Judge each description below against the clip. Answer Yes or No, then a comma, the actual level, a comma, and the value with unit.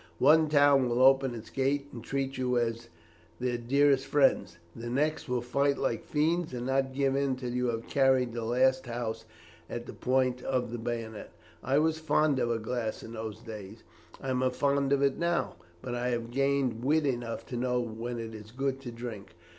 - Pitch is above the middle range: No, low, 125 Hz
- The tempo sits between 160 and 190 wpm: No, average, 200 wpm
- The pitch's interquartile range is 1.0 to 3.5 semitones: Yes, average, 2.7 semitones